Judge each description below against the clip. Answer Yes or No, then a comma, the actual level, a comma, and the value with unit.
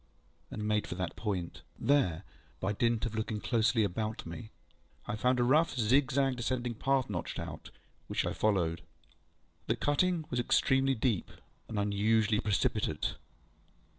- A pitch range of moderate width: Yes, average, 3.7 semitones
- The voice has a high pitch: No, low, 110 Hz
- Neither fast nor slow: Yes, average, 145 wpm